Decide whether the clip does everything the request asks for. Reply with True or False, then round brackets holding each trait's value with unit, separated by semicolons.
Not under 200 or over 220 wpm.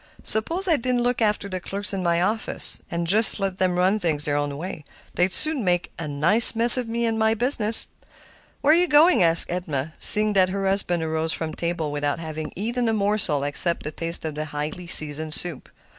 True (205 wpm)